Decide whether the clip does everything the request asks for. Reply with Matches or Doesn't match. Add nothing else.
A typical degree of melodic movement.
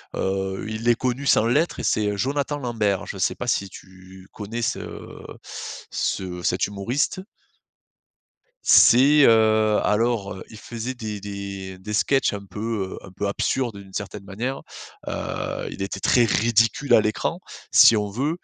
Matches